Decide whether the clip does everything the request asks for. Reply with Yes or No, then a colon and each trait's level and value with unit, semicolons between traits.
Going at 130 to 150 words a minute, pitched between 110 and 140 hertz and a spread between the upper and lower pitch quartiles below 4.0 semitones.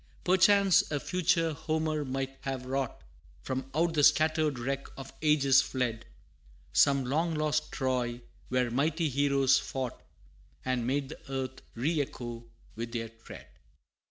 Yes: slow, 135 wpm; low, 135 Hz; average, 3.3 semitones